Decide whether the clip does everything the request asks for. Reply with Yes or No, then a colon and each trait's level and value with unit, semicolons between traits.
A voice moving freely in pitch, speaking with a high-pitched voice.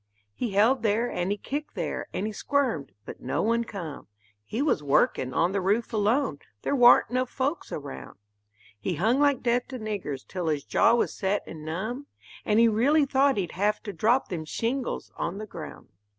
Yes: wide, 5.9 semitones; high, 215 Hz